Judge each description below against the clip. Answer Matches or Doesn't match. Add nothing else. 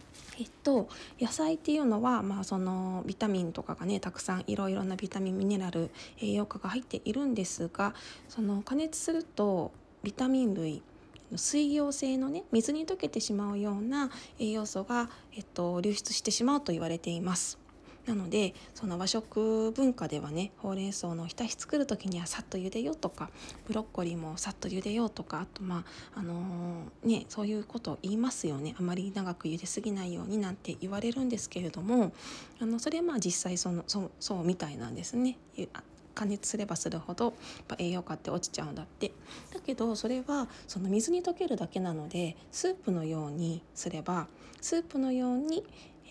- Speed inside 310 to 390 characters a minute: Matches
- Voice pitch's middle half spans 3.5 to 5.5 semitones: Matches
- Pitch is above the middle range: Matches